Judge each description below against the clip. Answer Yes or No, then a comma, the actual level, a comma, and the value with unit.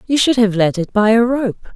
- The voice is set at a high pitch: Yes, high, 225 Hz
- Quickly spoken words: Yes, fast, 275 wpm